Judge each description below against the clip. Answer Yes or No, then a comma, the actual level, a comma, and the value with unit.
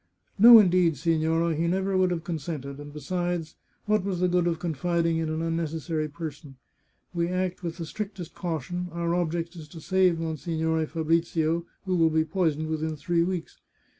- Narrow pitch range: Yes, narrow, 1.9 semitones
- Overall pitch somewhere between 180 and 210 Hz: No, medium, 165 Hz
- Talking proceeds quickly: No, average, 175 wpm